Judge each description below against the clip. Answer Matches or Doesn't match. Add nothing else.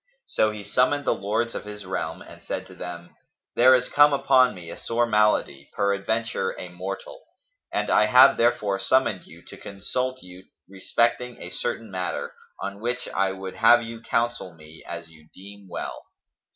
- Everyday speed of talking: Matches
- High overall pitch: Doesn't match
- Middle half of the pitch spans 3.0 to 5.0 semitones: Matches